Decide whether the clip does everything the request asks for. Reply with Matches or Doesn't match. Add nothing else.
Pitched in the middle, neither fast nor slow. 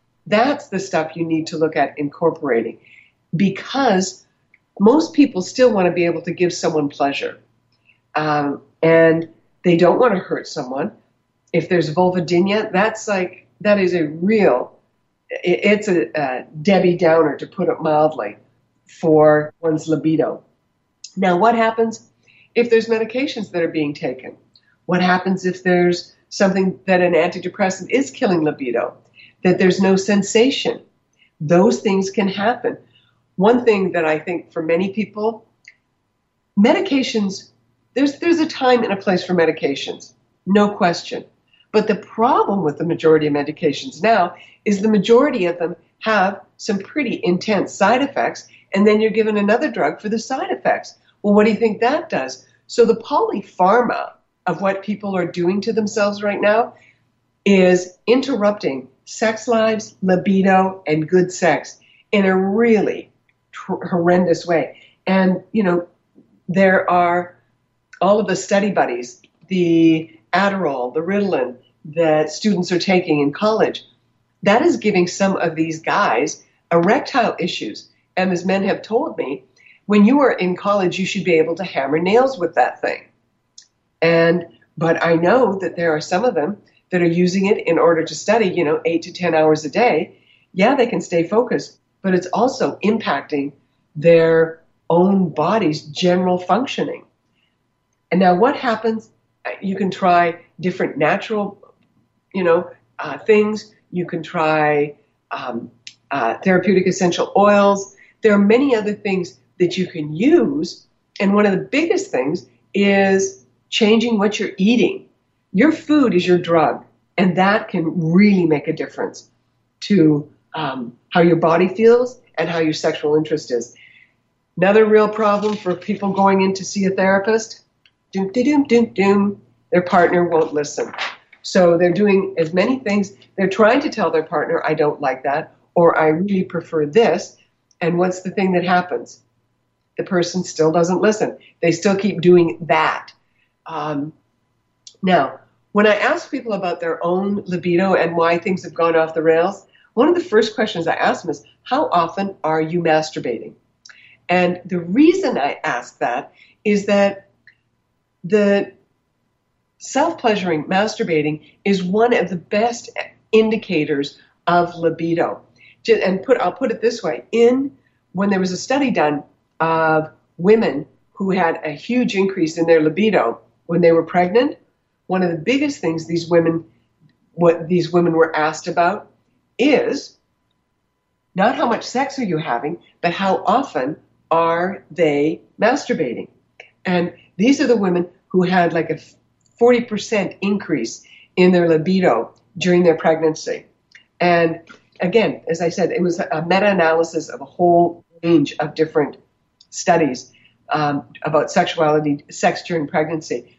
Matches